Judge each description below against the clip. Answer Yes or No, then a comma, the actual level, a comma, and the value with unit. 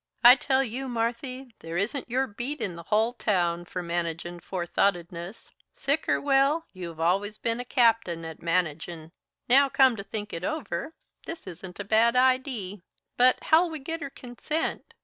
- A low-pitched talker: No, high, 225 Hz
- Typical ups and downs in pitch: No, wide, 7.1 semitones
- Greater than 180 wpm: No, average, 170 wpm